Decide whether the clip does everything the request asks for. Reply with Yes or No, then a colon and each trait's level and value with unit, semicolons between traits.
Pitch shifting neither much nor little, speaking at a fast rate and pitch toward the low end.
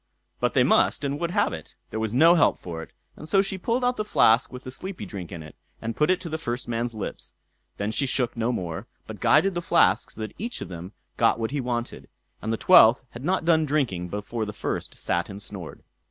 No: wide, 7.5 semitones; fast, 240 wpm; low, 120 Hz